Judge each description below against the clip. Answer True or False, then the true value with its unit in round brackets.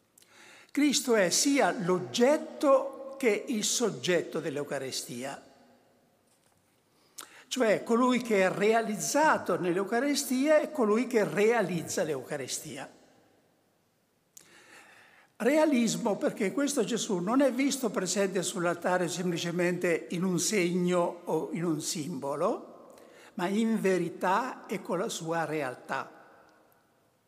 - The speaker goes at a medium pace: False (95 wpm)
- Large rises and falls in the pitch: True (6.8 semitones)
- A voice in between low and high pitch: False (215 Hz)